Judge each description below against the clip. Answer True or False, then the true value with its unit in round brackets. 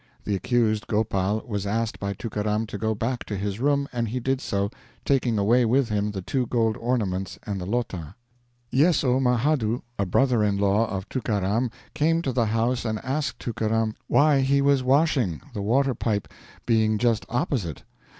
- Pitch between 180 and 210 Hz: False (115 Hz)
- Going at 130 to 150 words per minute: False (175 wpm)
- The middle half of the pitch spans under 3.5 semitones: False (3.8 semitones)